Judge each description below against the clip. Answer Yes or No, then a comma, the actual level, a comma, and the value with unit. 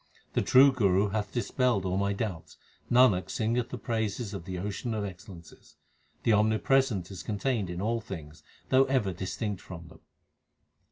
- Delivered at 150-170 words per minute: Yes, average, 160 wpm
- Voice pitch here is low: Yes, low, 105 Hz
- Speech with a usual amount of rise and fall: Yes, average, 4.0 semitones